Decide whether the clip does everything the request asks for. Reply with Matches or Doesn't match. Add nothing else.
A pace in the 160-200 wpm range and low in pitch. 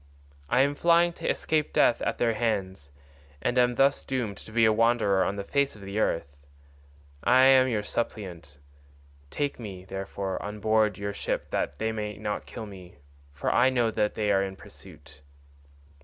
Matches